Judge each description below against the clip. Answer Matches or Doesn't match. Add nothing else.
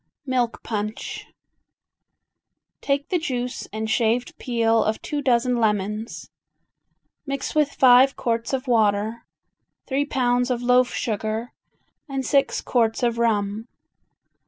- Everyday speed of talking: Doesn't match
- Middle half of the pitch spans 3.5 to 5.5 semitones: Doesn't match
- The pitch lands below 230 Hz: Doesn't match